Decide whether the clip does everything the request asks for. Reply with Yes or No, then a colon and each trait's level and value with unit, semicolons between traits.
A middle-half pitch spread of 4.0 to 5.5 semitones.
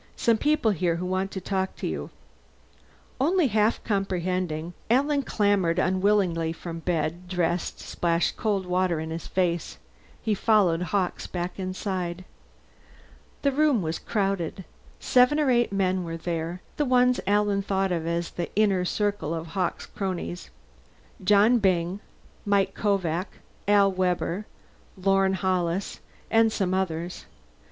No: average, 3.0 semitones